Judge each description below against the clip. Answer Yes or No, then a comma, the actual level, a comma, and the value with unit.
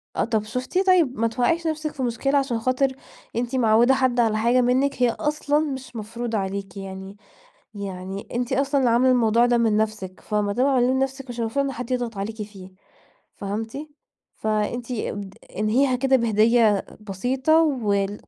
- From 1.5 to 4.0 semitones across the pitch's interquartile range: Yes, average, 3.7 semitones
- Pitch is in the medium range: No, high, 240 Hz